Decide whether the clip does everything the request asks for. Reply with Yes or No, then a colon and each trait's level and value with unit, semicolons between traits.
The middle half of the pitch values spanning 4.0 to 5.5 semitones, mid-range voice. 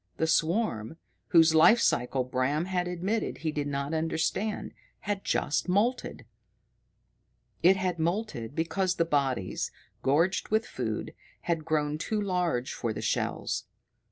Yes: average, 4.5 semitones; medium, 165 Hz